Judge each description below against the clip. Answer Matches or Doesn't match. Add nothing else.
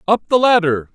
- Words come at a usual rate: Matches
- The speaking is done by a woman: Doesn't match